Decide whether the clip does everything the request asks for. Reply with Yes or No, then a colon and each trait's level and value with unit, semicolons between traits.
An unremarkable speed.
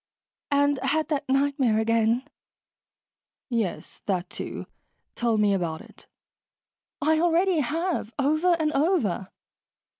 No: slow, 110 wpm